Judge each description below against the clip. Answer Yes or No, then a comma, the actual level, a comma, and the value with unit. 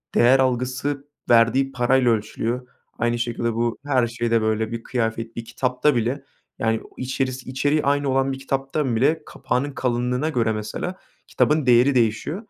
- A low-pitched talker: Yes, low, 125 Hz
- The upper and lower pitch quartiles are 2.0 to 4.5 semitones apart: Yes, narrow, 2.6 semitones